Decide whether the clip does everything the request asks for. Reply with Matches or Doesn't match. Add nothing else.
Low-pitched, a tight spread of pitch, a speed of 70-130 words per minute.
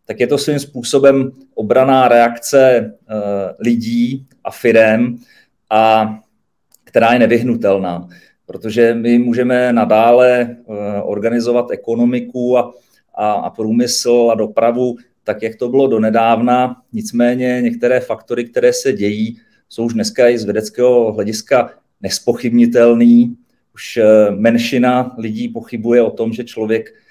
Matches